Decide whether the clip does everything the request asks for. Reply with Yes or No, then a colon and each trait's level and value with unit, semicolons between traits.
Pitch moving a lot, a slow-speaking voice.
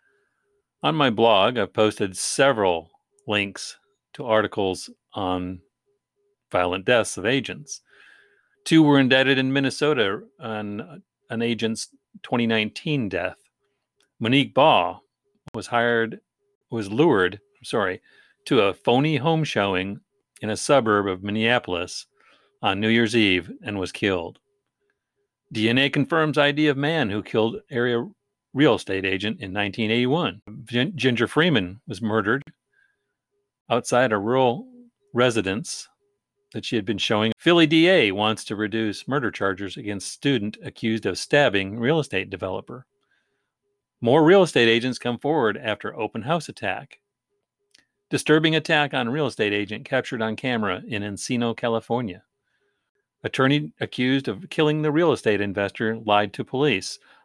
Yes: wide, 6.9 semitones; slow, 130 wpm